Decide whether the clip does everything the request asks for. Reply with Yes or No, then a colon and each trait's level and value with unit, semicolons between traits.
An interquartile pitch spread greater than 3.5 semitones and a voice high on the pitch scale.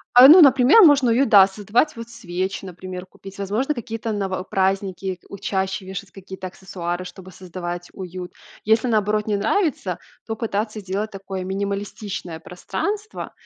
No: average, 3.2 semitones; high, 195 Hz